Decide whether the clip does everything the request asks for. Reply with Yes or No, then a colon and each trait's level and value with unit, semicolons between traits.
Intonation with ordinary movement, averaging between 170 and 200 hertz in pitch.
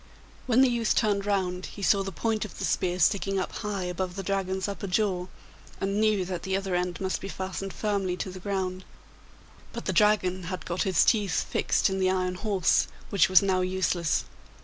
No: narrow, 1.6 semitones; high, 190 Hz